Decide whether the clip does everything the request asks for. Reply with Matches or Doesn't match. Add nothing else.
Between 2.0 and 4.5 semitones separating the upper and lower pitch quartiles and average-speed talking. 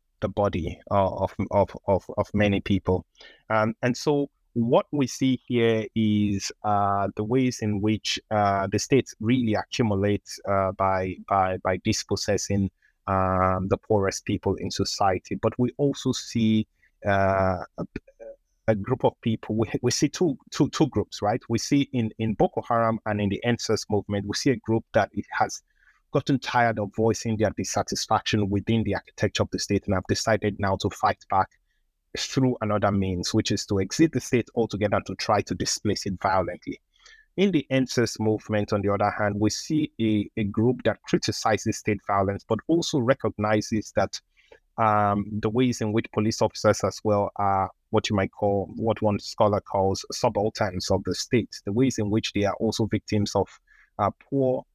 Matches